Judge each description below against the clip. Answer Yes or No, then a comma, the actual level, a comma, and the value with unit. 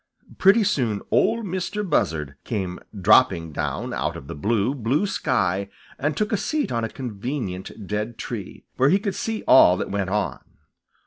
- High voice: No, low, 115 Hz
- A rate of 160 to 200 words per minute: Yes, average, 170 wpm